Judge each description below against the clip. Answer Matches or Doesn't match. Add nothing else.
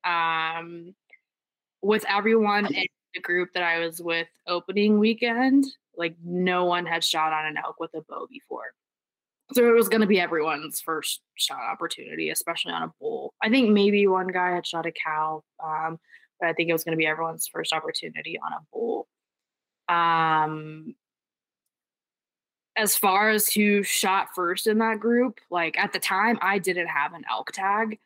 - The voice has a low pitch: Doesn't match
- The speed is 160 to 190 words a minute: Matches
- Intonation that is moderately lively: Matches